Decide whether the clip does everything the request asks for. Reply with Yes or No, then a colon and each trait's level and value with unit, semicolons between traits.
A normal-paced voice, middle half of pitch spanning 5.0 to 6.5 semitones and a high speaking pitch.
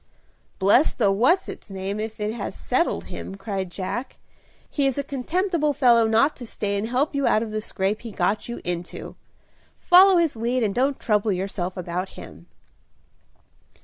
Yes: average, 175 wpm; wide, 5.5 semitones; high, 220 Hz